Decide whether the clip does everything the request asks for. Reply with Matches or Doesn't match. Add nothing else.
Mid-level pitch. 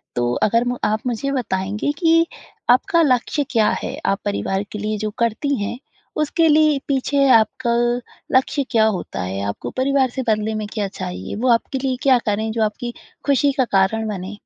Doesn't match